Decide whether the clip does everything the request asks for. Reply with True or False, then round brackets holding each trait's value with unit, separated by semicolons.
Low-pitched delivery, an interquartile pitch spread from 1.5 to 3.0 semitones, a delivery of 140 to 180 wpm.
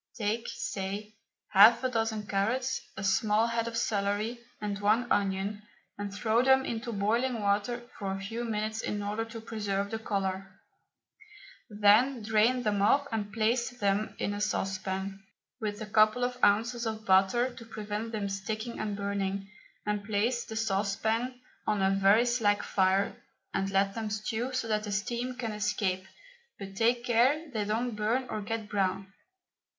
False (215 Hz; 2.4 semitones; 165 wpm)